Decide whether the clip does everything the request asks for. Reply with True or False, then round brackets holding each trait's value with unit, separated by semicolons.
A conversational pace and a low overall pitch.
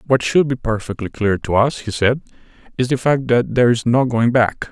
False (230 wpm; 120 Hz)